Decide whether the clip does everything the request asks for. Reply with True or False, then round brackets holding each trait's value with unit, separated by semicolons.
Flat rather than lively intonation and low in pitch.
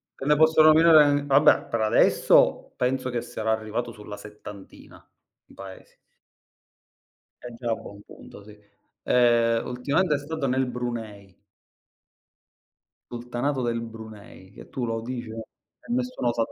False (3.7 semitones; 120 Hz)